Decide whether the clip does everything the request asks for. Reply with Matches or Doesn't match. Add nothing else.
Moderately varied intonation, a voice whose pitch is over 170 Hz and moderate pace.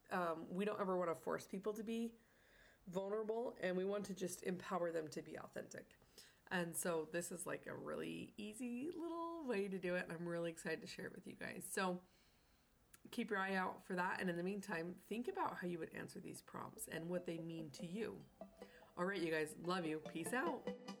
Doesn't match